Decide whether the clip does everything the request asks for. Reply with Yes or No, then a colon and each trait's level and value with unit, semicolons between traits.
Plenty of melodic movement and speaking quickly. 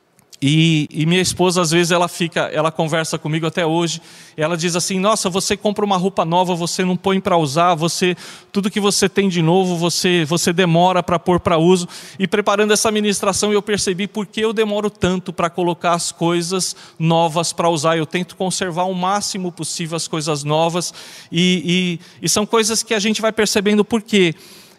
No: average, 2.7 semitones; fast, 195 wpm